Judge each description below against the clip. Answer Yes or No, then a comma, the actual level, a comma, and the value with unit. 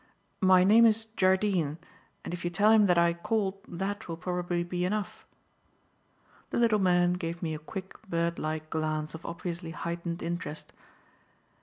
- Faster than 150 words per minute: Yes, average, 160 wpm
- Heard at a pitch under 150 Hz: No, medium, 175 Hz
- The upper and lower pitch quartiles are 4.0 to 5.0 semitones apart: No, narrow, 2.4 semitones